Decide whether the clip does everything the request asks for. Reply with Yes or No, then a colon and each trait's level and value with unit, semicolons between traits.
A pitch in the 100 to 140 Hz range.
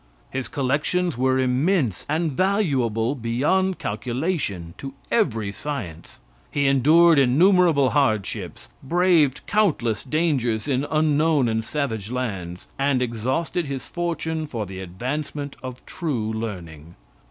Yes: low, 135 Hz